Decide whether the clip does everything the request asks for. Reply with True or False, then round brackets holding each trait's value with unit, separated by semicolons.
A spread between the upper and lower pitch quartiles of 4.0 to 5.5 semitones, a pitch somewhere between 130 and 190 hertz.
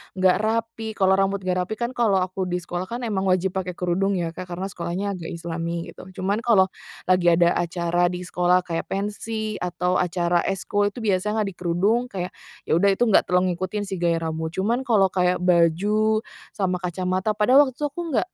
False (2.9 semitones; 185 Hz)